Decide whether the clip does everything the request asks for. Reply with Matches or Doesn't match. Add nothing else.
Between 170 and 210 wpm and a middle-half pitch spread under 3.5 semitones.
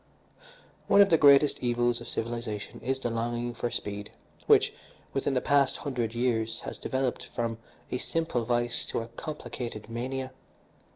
Doesn't match